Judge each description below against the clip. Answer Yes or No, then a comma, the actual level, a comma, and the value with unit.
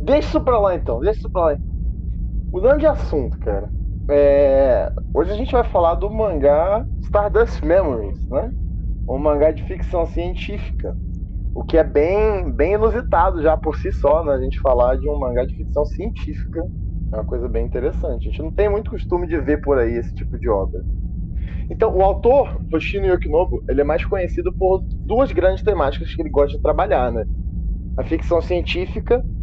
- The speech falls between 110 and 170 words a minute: No, fast, 185 wpm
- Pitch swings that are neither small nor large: No, wide, 8.5 semitones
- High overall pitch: No, medium, 165 Hz